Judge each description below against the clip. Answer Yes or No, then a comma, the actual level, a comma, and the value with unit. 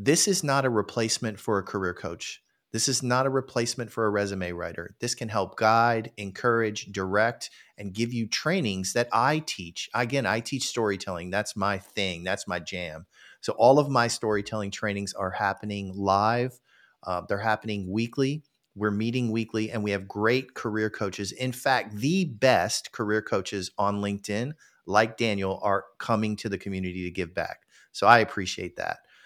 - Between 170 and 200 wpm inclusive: Yes, average, 175 wpm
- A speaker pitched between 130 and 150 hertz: No, low, 105 Hz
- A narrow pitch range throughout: No, average, 3.1 semitones